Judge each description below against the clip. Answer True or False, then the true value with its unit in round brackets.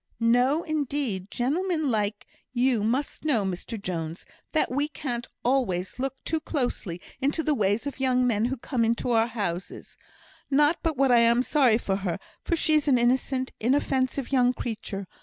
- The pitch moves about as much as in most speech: True (4.2 semitones)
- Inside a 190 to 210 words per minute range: False (160 wpm)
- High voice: True (250 Hz)